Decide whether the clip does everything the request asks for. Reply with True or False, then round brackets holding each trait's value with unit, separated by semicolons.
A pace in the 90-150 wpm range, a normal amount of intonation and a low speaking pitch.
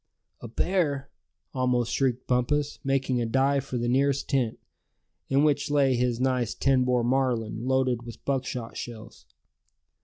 False (145 wpm; 2.1 semitones; 130 Hz)